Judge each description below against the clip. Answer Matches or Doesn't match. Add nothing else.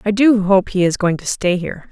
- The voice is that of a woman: Matches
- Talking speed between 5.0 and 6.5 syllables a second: Matches